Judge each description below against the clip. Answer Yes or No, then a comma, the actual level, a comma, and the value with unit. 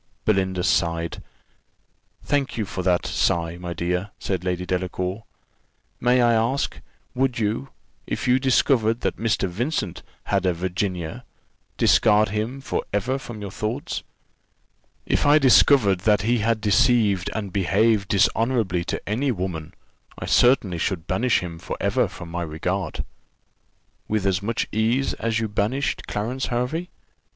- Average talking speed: Yes, average, 145 wpm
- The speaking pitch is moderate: No, low, 105 Hz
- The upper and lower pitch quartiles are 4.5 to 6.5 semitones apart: Yes, average, 4.8 semitones